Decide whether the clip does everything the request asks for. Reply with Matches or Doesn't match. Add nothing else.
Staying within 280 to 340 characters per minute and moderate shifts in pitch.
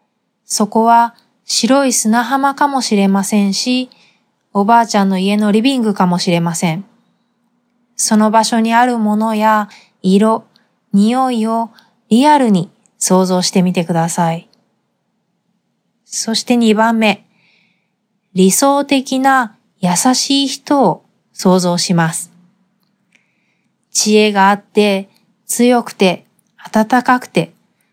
Doesn't match